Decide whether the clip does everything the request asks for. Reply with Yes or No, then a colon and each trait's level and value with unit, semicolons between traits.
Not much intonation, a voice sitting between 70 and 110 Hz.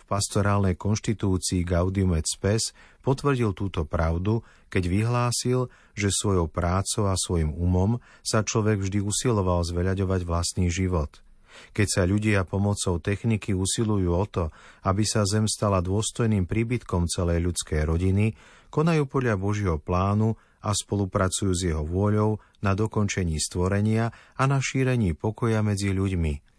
No: average, 3.2 semitones; low, 100 Hz